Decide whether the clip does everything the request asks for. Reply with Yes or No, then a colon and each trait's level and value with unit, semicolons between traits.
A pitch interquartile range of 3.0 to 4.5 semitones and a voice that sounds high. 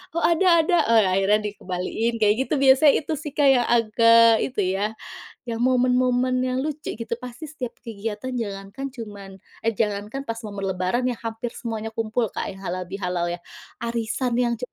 Yes: average, 3.4 semitones; high, 230 Hz